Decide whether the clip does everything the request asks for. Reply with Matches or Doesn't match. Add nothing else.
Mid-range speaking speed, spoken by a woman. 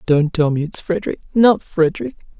Matches